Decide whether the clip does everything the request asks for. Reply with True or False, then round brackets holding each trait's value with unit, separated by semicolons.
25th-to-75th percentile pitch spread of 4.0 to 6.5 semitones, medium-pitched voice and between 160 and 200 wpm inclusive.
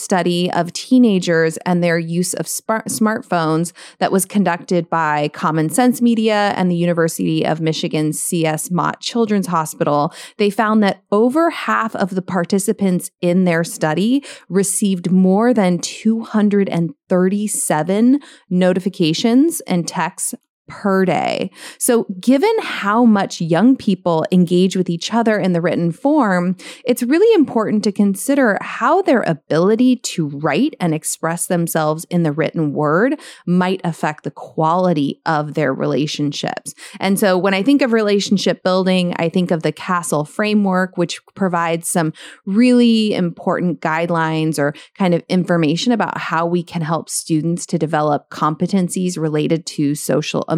False (4.4 semitones; 180 Hz; 140 wpm)